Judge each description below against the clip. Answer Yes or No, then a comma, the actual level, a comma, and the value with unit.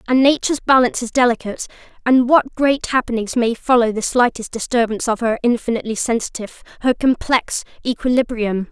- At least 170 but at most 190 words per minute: No, average, 145 wpm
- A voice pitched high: Yes, high, 240 Hz